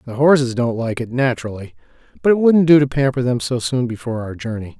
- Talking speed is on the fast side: Yes, fast, 225 wpm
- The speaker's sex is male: Yes, male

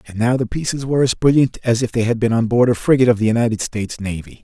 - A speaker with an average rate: No, fast, 285 wpm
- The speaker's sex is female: No, male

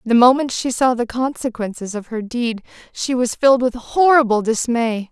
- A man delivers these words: No, female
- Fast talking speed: No, average, 175 wpm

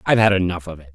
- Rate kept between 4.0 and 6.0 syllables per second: No, 8.4 syllables/s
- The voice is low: Yes, very low, 90 Hz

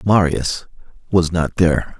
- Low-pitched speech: Yes, very low, 85 Hz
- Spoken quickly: No, slow, 120 wpm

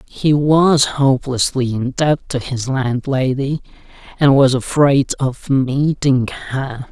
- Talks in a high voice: No, low, 135 Hz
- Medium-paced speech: No, slow, 120 wpm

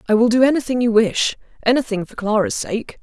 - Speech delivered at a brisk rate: No, average, 180 wpm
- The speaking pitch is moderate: No, high, 230 Hz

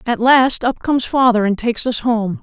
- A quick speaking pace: Yes, fast, 225 wpm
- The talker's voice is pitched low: No, high, 235 Hz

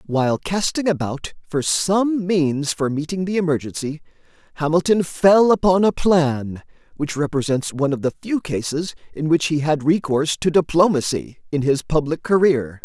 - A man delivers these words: Yes, male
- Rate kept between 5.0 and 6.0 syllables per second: No, 4.8 syllables/s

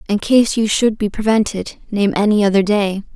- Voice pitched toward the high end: Yes, high, 210 Hz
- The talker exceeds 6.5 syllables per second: No, 5.1 syllables/s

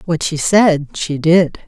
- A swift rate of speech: No, average, 180 wpm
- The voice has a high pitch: No, medium, 165 Hz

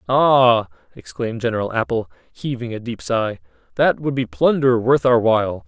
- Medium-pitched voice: No, low, 115 Hz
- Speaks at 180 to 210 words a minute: No, average, 160 wpm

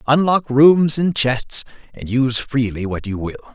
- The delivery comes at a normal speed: Yes, average, 170 wpm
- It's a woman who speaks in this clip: No, male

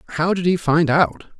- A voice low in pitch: No, medium, 160 Hz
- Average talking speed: No, fast, 215 wpm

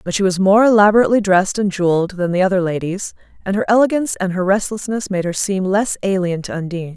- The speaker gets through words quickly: Yes, fast, 215 wpm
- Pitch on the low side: No, high, 195 Hz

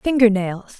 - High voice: Yes, high, 215 Hz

